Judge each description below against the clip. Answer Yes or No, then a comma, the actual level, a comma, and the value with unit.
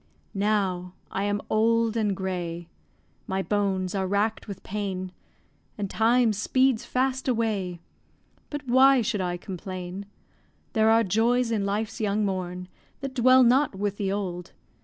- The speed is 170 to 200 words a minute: No, average, 140 wpm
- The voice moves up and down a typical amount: Yes, average, 3.4 semitones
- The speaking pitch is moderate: No, high, 205 Hz